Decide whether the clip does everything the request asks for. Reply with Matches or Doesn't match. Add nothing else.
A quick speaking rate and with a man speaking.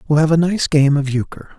Matches